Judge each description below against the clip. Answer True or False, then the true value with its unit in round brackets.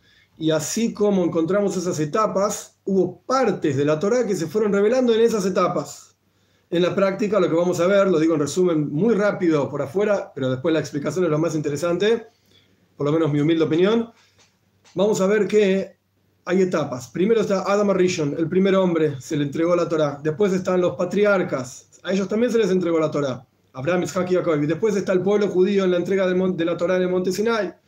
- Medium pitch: True (180 Hz)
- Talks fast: True (210 wpm)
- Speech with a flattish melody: False (4.6 semitones)